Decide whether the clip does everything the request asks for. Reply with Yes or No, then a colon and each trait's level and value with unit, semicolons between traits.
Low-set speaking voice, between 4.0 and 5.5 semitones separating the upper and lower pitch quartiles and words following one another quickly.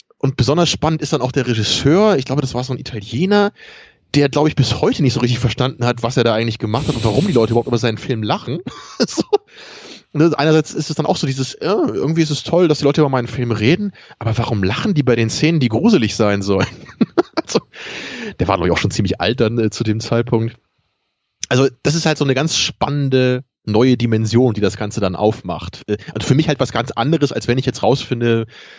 Yes: low, 125 Hz; average, 4.6 semitones; fast, 235 wpm